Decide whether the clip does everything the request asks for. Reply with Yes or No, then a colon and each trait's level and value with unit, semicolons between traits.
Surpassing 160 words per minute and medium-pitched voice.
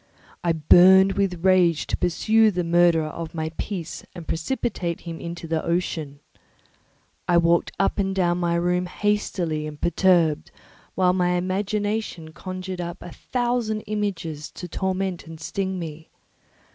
No: average, 145 wpm; medium, 175 Hz